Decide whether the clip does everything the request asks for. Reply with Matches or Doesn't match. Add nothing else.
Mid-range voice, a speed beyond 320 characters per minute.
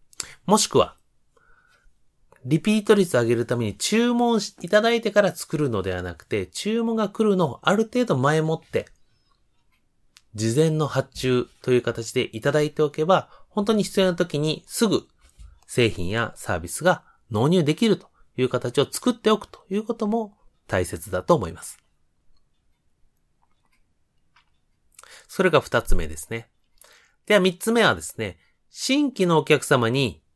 Doesn't match